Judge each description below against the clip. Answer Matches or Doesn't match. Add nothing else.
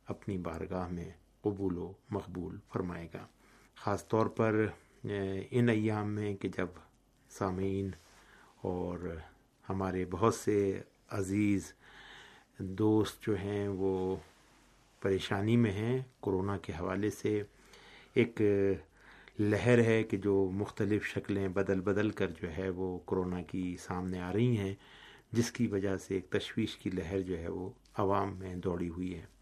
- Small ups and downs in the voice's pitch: Matches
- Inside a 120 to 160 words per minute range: Matches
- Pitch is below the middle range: Matches